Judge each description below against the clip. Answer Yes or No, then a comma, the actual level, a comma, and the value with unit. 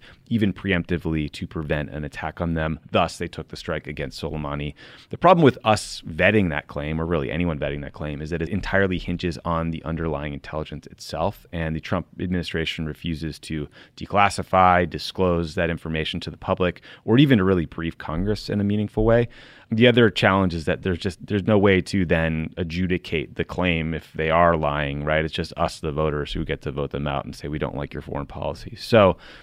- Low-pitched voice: Yes, very low, 85 Hz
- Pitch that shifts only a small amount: No, average, 3.3 semitones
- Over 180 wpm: Yes, fast, 205 wpm